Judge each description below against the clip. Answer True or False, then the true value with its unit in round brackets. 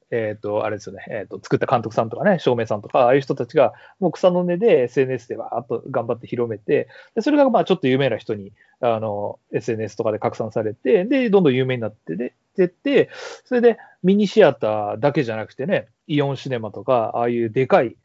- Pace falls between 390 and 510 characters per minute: True (425 characters per minute)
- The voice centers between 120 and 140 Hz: True (135 Hz)